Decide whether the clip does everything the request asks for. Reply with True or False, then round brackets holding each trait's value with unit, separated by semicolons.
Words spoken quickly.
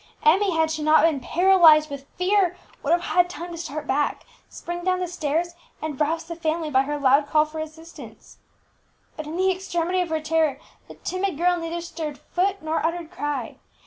False (195 wpm)